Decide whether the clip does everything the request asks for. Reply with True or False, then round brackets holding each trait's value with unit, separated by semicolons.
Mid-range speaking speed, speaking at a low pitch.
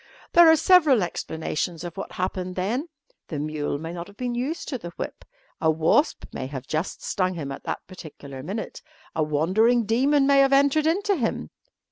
False (185 wpm; 195 Hz)